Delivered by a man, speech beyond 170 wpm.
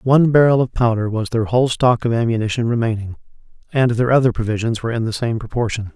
Yes: male; average, 200 wpm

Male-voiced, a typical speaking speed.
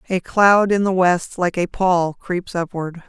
No: female; average, 195 wpm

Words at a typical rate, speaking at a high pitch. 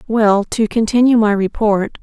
Yes: average, 150 wpm; high, 215 Hz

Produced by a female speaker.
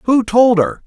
Yes: female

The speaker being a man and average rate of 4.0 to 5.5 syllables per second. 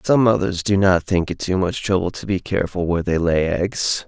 Yes: male; 5.3 syllables/s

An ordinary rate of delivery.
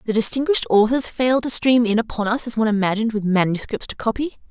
No: fast, 215 wpm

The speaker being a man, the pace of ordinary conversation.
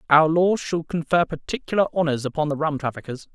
Yes: male; average, 180 wpm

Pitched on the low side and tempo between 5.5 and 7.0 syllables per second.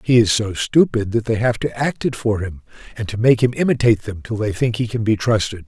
Yes: low, 115 Hz; 5.8 syllables/s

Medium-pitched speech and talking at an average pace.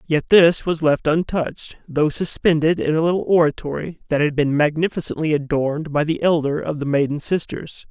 Yes: medium, 155 Hz; average, 175 wpm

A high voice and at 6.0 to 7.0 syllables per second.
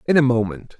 No: low, 125 Hz; 6.6 syllables/s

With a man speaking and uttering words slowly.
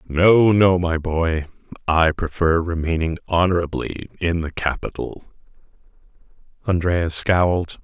Yes: male; slow, 100 wpm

